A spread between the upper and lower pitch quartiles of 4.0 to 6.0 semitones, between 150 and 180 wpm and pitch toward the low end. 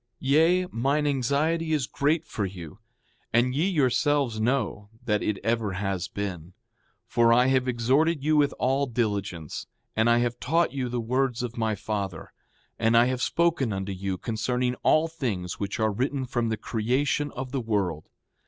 Yes: average, 4.8 semitones; average, 170 wpm; low, 120 Hz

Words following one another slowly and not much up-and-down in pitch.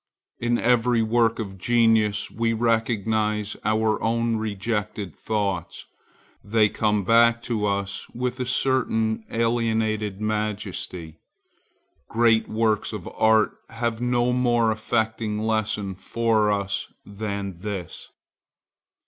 Yes: slow, 105 wpm; narrow, 1.8 semitones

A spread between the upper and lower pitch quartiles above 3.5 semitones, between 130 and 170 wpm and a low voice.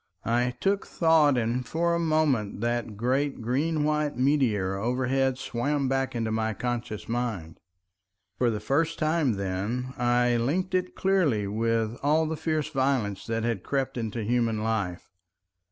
Yes: average, 4.7 semitones; average, 150 wpm; low, 125 Hz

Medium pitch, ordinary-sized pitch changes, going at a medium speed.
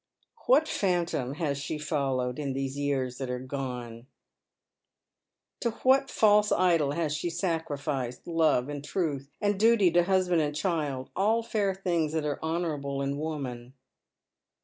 Yes: medium, 150 Hz; average, 4.6 semitones; average, 145 wpm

